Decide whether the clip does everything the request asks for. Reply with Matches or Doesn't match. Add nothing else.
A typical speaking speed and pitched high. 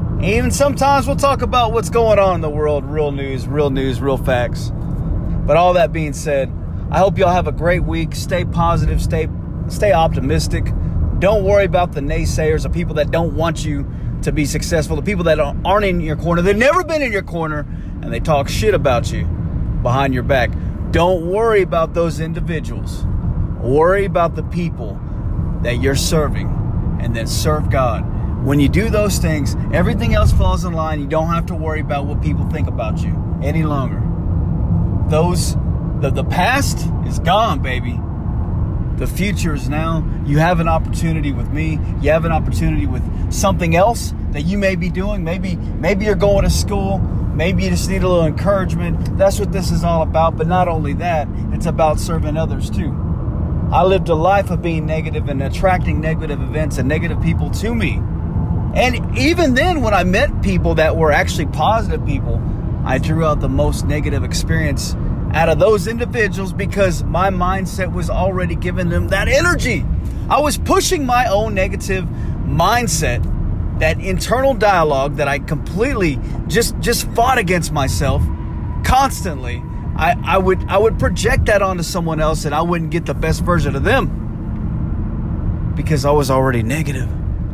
Doesn't match